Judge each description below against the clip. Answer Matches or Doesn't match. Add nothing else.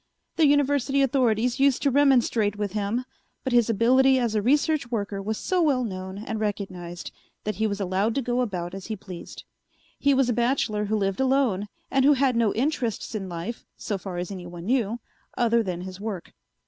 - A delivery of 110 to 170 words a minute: Doesn't match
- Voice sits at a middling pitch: Doesn't match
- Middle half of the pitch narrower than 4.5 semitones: Doesn't match